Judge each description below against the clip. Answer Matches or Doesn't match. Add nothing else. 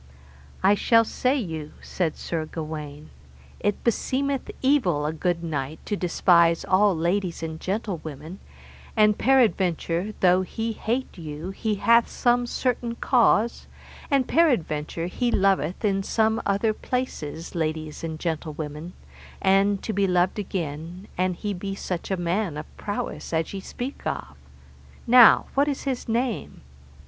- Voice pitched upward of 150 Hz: Matches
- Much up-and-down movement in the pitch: Matches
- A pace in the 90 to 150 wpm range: Matches